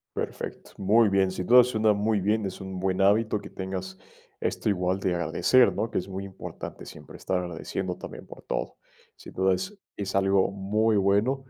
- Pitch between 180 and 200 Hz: No, very low, 95 Hz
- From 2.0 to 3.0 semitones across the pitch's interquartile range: Yes, narrow, 2.4 semitones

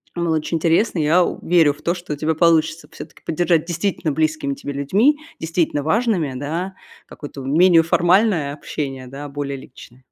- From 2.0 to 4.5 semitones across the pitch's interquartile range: Yes, average, 3.2 semitones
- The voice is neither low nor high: Yes, medium, 160 Hz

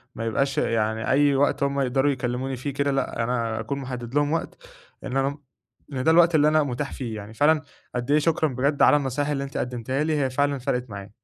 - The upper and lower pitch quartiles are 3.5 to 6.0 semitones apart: No, average, 2.8 semitones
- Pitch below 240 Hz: Yes, low, 135 Hz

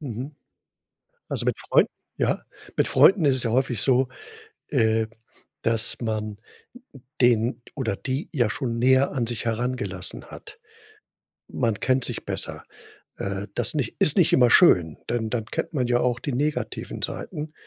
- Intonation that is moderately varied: Yes, average, 3.2 semitones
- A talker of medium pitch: No, low, 120 Hz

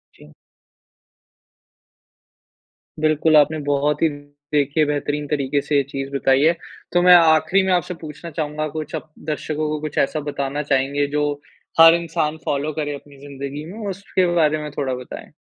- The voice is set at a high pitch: No, medium, 150 Hz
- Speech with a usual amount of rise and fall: No, narrow, 1.8 semitones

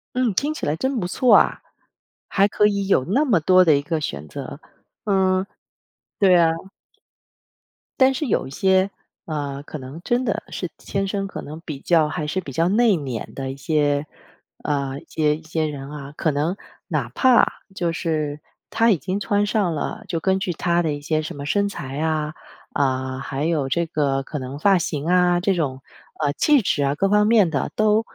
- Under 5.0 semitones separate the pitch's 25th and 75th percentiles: No, average, 5.3 semitones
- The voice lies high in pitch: No, medium, 165 Hz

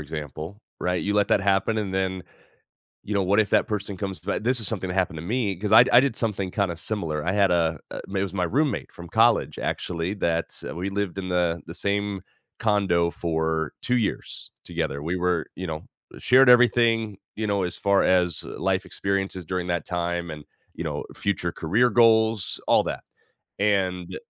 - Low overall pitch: Yes, very low, 95 Hz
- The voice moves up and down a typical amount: Yes, average, 3.1 semitones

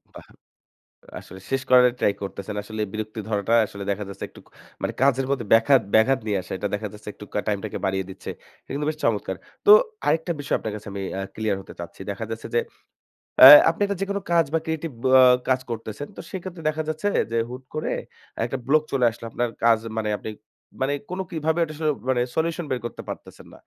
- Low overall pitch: Yes, low, 120 Hz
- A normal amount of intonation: No, wide, 6.6 semitones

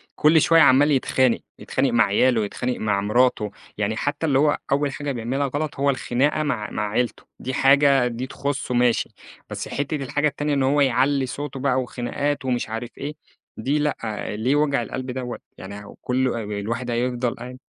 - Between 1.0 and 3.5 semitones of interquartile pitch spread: Yes, average, 2.9 semitones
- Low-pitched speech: Yes, low, 130 Hz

